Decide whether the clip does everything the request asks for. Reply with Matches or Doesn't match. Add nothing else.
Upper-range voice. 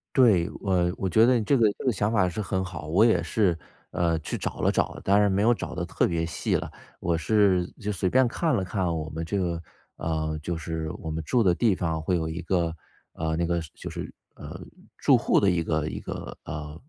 Doesn't match